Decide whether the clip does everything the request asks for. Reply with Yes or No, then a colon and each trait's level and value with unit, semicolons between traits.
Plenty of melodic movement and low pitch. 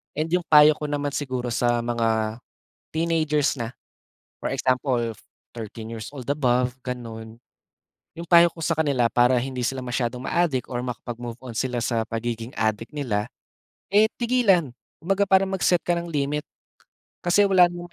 Yes: wide, 5.7 semitones; low, 130 Hz